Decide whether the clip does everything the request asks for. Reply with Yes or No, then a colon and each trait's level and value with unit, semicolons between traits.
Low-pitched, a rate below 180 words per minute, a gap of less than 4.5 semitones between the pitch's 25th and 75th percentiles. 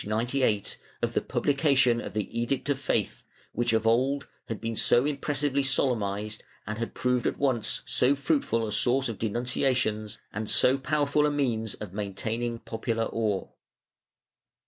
Yes: low, 120 Hz; average, 155 wpm; average, 3.8 semitones